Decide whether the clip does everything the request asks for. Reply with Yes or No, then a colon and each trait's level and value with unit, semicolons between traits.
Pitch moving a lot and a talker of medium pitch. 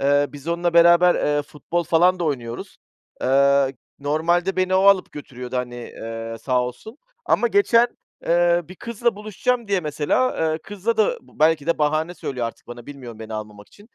Yes: wide, 6.0 semitones; medium, 155 Hz